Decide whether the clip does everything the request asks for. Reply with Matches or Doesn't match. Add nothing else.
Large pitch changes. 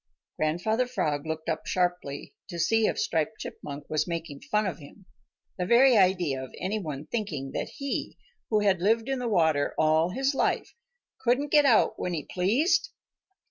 Matches